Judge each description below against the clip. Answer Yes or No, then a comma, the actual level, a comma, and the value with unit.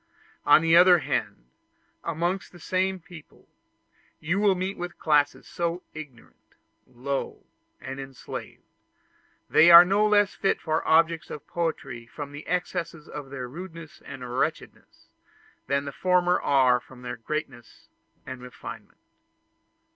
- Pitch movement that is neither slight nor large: Yes, average, 4.8 semitones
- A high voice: No, medium, 160 Hz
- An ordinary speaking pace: No, slow, 130 wpm